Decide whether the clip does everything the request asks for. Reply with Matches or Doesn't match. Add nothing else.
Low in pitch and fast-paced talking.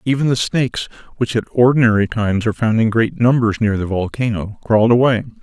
Doesn't match